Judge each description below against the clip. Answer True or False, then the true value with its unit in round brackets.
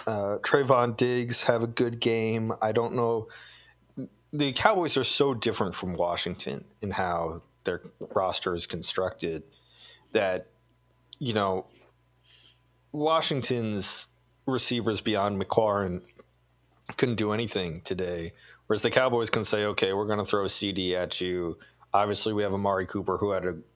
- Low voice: True (110 Hz)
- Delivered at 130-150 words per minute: True (140 wpm)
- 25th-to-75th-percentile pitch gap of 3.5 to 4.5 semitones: True (4.2 semitones)